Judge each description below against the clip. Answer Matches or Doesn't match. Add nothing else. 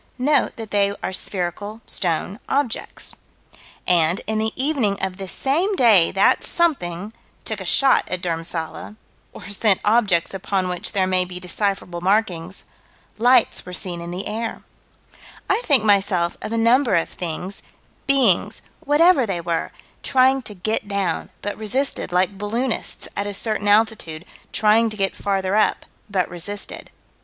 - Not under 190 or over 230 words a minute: Doesn't match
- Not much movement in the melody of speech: Doesn't match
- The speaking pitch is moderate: Doesn't match